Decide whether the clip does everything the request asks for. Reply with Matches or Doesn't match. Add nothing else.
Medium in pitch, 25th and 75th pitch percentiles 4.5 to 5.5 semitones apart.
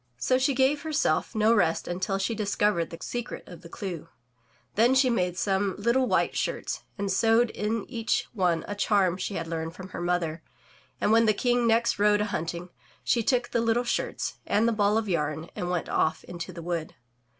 Doesn't match